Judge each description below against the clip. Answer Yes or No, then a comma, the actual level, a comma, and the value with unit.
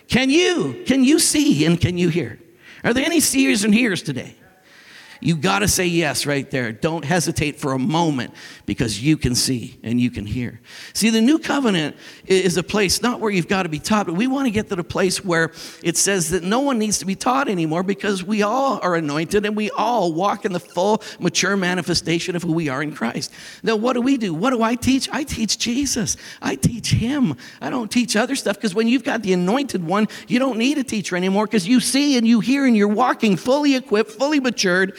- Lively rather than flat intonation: Yes, wide, 6.3 semitones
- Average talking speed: No, fast, 230 wpm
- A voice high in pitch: Yes, high, 205 Hz